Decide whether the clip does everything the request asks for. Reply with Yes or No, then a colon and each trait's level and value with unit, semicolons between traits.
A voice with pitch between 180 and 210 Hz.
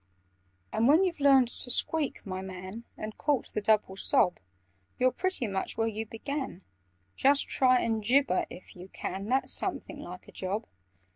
No: high, 225 Hz